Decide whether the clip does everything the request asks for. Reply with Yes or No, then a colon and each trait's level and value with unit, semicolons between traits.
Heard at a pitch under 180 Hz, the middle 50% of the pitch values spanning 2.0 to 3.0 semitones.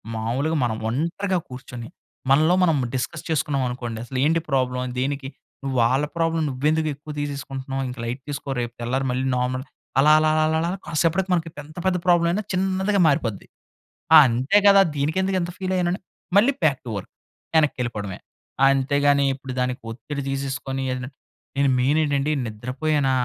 No: medium, 140 Hz; average, 3.8 semitones